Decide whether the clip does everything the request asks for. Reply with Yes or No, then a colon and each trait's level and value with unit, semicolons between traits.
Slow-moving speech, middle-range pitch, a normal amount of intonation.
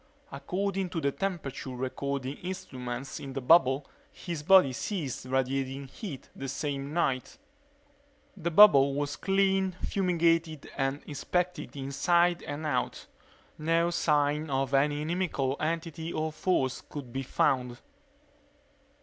Yes: slow, 120 wpm; medium, 145 Hz; average, 4.1 semitones